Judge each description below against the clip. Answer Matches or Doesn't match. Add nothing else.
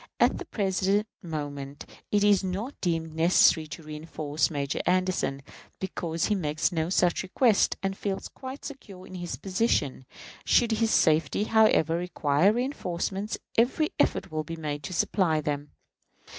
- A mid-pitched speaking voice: Matches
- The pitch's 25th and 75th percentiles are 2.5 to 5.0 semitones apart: Matches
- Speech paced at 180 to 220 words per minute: Doesn't match